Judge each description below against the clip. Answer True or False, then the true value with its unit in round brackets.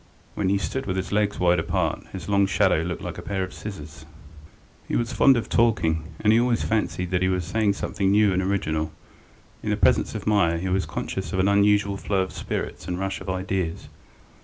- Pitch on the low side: True (95 Hz)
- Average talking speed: False (215 wpm)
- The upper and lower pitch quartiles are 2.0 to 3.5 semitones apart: True (2.4 semitones)